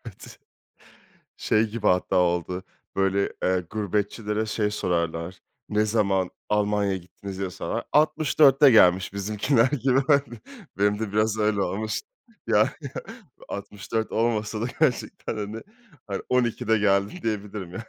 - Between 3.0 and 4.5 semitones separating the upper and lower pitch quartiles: No, narrow, 2.5 semitones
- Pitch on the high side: No, low, 105 Hz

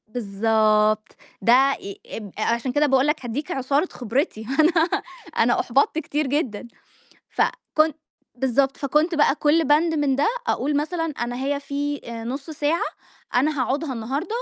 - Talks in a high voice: Yes, very high, 275 Hz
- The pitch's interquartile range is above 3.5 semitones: Yes, average, 3.9 semitones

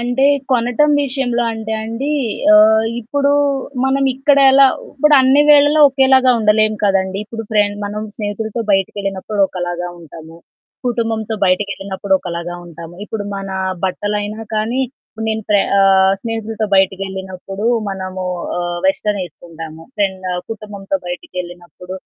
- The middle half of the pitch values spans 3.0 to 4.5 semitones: Yes, average, 3.5 semitones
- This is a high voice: Yes, high, 210 Hz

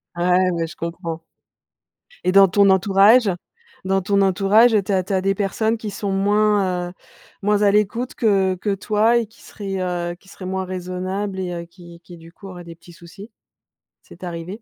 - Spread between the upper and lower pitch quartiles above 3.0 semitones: No, narrow, 2.4 semitones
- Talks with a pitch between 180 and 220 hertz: Yes, high, 190 Hz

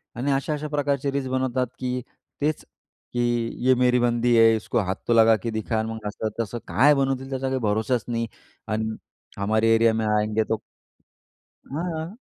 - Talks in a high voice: No, low, 120 Hz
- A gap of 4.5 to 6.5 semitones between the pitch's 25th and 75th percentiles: No, average, 3.1 semitones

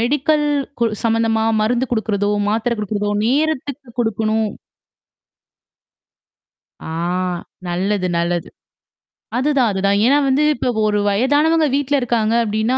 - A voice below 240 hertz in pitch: Yes, high, 230 Hz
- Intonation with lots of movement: No, average, 4.2 semitones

